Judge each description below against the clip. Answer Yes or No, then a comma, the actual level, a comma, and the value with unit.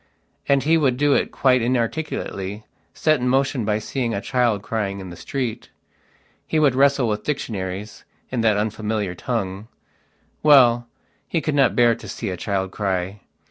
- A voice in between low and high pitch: No, low, 115 Hz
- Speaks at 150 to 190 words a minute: Yes, average, 165 wpm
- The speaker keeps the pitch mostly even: No, average, 4.8 semitones